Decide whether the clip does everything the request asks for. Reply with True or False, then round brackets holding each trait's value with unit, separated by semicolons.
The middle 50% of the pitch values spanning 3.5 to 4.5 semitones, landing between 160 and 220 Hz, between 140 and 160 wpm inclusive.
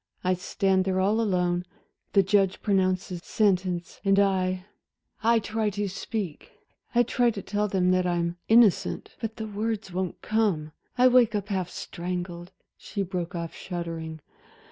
False (2.8 semitones; 190 Hz; 150 wpm)